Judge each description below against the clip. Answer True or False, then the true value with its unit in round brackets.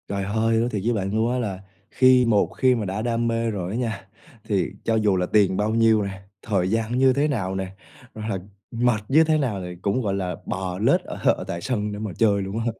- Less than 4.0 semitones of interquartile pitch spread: True (3.1 semitones)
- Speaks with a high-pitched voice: False (110 Hz)